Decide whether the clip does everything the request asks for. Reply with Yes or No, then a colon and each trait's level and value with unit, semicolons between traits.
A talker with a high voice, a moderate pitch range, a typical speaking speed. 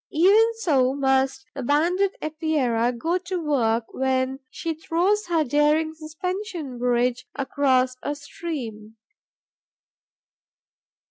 No: very high, 290 Hz; average, 4.7 semitones; slow, 105 wpm